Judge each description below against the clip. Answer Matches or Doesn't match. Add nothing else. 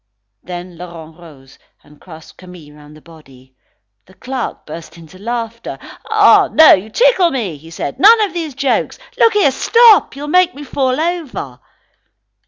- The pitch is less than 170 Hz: Doesn't match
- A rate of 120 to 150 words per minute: Doesn't match